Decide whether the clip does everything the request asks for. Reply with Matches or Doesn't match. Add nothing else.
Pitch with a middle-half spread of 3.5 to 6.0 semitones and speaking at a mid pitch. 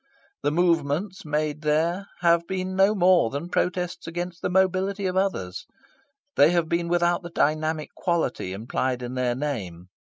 Matches